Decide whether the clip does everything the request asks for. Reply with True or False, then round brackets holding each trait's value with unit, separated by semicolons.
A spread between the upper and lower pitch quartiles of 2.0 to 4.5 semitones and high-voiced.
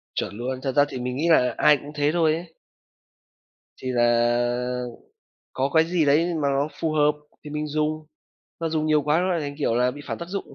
False (3.8 semitones; 145 Hz)